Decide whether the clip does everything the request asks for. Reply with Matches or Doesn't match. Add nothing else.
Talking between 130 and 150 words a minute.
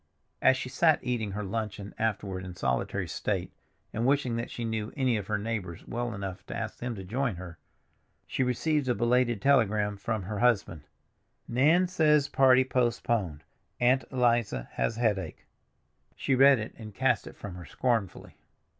Doesn't match